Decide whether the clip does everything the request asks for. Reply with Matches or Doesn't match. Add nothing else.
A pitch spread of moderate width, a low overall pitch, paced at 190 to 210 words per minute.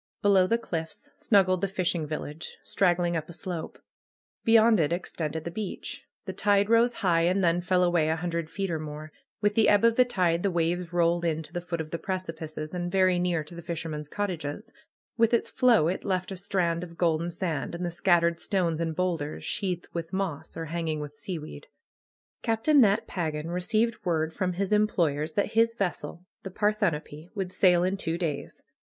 Doesn't match